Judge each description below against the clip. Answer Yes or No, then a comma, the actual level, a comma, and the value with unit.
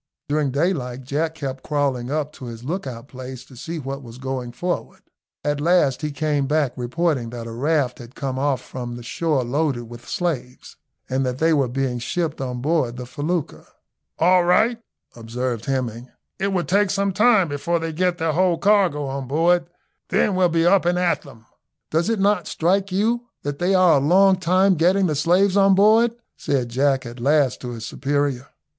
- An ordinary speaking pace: Yes, average, 190 wpm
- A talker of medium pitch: Yes, medium, 145 Hz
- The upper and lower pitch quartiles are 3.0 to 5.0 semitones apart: No, wide, 5.6 semitones